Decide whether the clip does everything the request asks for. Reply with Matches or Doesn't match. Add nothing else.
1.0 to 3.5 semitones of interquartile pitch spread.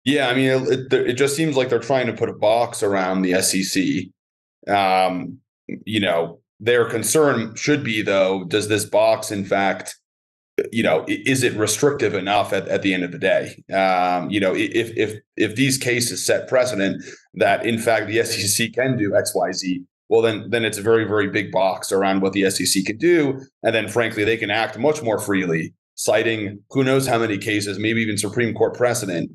Doesn't match